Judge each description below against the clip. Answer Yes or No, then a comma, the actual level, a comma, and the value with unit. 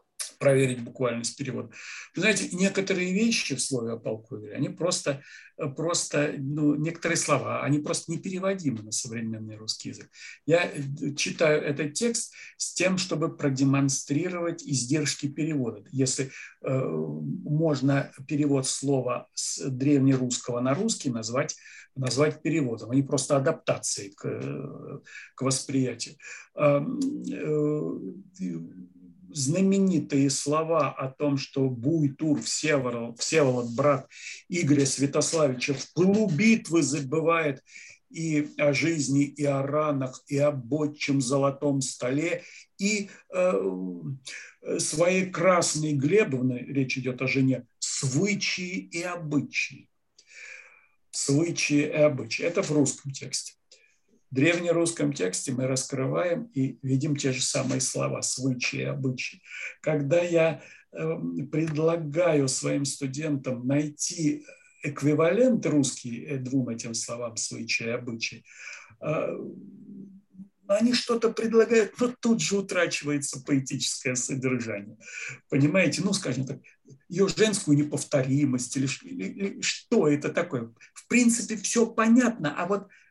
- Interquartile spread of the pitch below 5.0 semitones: Yes, average, 4.2 semitones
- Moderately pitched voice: Yes, medium, 145 Hz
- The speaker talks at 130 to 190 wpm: No, slow, 110 wpm